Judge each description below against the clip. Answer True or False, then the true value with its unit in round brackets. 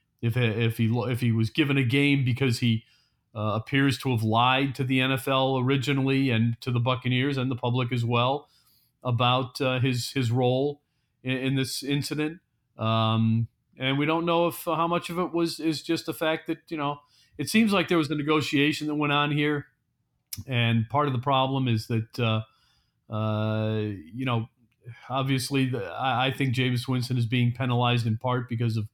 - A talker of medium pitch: False (130 Hz)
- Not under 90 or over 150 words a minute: False (190 wpm)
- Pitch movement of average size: True (3.1 semitones)